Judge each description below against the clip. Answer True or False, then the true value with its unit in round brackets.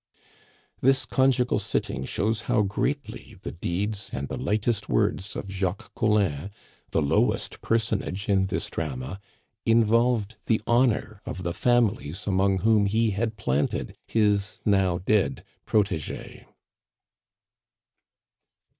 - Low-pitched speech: True (105 Hz)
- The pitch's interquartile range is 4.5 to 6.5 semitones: False (2.9 semitones)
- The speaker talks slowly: True (115 wpm)